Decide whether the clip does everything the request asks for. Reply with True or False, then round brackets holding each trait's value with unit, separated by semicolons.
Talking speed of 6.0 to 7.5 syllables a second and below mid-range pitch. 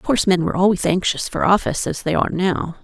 False (7.0 syllables/s; 185 Hz)